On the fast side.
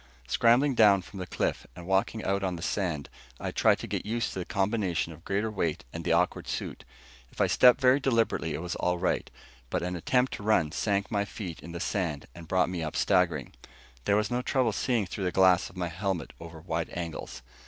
Yes: fast, 220 wpm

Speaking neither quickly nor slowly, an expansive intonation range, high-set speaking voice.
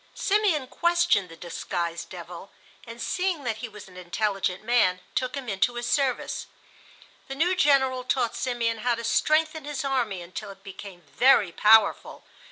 Yes: average, 160 wpm; wide, 5.8 semitones; high, 235 Hz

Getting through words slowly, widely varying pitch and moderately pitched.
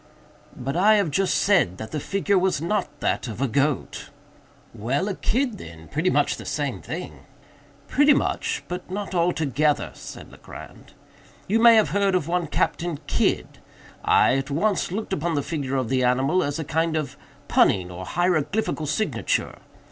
No: average, 165 wpm; wide, 6.0 semitones; medium, 165 Hz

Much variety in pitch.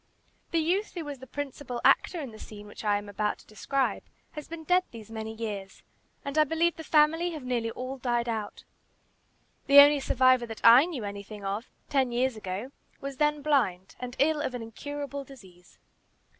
No: average, 5.0 semitones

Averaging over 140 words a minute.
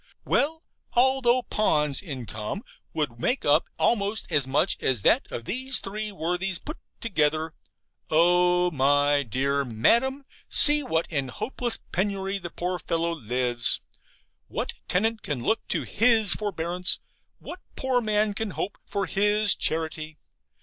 No: slow, 135 wpm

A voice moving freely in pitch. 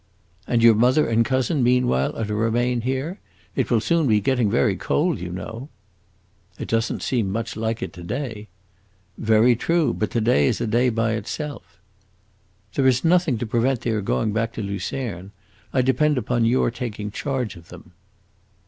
No: average, 3.2 semitones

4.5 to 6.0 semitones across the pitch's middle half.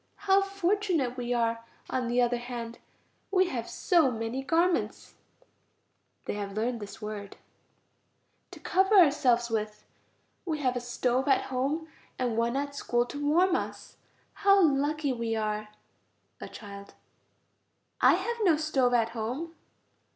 Yes: wide, 5.6 semitones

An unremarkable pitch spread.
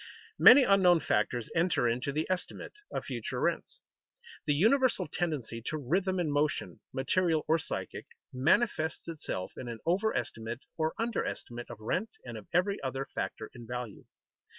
No: wide, 7.0 semitones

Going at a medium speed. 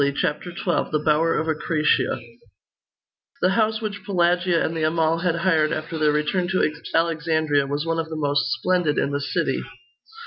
Yes: average, 170 wpm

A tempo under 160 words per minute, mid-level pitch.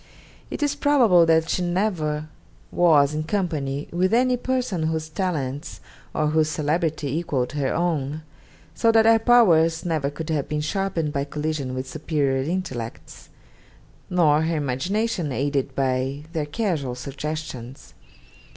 Yes: slow, 135 wpm; medium, 155 Hz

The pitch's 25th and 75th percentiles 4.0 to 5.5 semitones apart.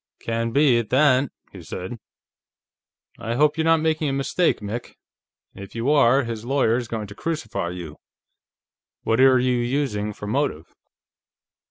Yes: average, 4.4 semitones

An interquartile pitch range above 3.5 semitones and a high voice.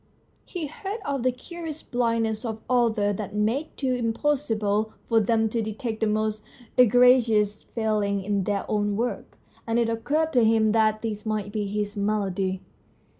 No: average, 2.7 semitones; high, 220 Hz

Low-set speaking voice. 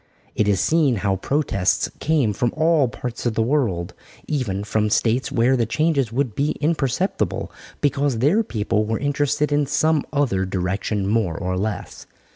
Yes: low, 120 Hz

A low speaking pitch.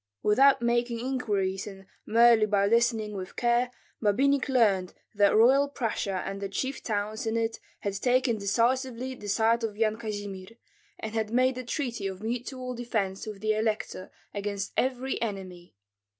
No: high, 225 Hz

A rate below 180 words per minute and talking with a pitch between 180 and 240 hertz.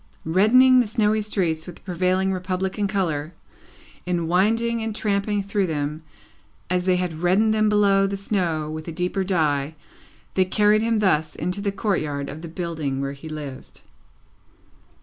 Yes: average, 160 wpm; medium, 185 Hz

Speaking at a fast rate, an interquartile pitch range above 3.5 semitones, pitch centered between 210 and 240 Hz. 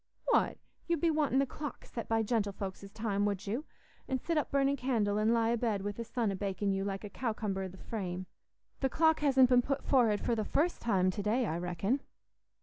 Yes: fast, 225 wpm; average, 4.9 semitones; high, 225 Hz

